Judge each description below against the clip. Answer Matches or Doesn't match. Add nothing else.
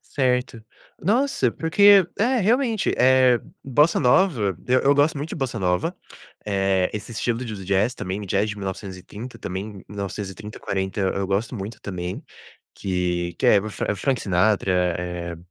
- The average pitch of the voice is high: Doesn't match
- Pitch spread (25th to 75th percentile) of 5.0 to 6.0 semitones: Matches